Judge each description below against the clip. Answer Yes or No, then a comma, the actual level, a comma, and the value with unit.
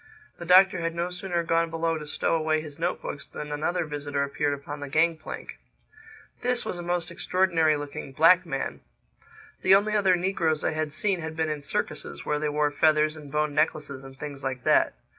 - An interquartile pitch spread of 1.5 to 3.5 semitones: Yes, average, 2.7 semitones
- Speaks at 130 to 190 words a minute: No, average, 200 wpm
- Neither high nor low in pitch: Yes, medium, 155 Hz